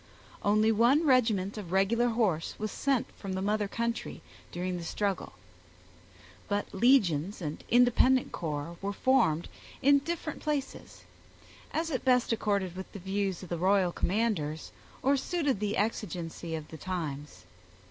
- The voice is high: Yes, high, 205 Hz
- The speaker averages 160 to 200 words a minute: No, average, 145 wpm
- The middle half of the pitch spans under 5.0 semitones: No, wide, 5.5 semitones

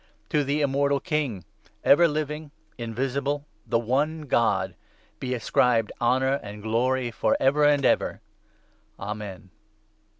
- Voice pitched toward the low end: Yes, low, 130 Hz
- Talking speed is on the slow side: Yes, slow, 125 wpm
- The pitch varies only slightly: No, average, 3.9 semitones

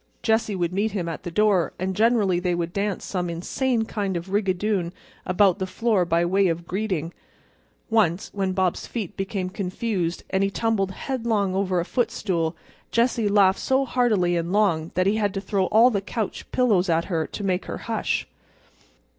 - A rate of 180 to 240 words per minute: Yes, average, 190 wpm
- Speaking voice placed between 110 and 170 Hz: No, high, 195 Hz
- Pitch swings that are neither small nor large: Yes, average, 3.3 semitones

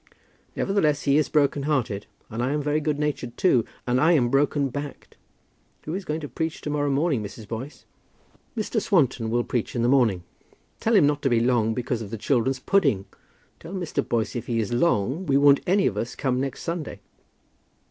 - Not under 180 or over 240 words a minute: Yes, average, 200 wpm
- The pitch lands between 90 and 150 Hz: Yes, medium, 140 Hz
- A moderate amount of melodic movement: Yes, average, 4.1 semitones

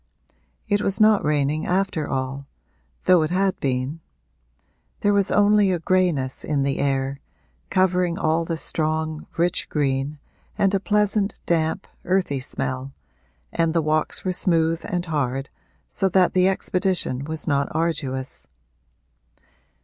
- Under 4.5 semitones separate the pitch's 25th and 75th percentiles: No, average, 4.8 semitones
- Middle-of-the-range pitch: Yes, medium, 165 Hz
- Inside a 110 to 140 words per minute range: Yes, slow, 135 wpm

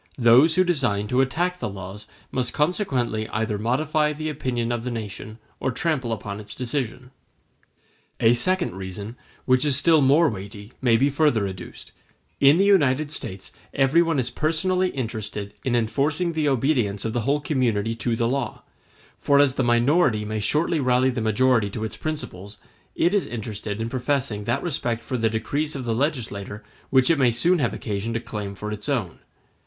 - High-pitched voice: No, low, 125 Hz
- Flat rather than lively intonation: No, average, 5.1 semitones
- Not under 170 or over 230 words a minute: Yes, average, 180 wpm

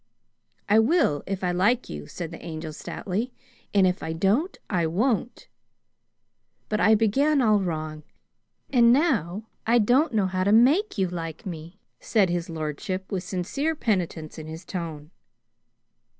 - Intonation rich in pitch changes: Yes, wide, 5.7 semitones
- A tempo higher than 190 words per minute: No, average, 150 wpm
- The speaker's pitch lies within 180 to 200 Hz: Yes, high, 190 Hz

